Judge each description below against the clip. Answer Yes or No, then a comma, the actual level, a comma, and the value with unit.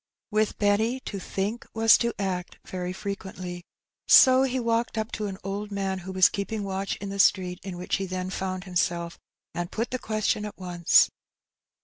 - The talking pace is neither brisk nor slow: Yes, average, 180 wpm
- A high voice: Yes, high, 195 Hz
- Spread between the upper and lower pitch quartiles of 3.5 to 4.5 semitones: No, average, 2.7 semitones